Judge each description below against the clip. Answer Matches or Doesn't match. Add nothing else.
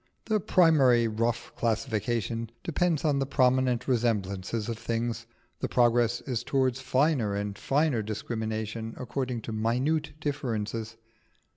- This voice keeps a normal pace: Doesn't match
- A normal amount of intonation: Matches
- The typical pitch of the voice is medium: Doesn't match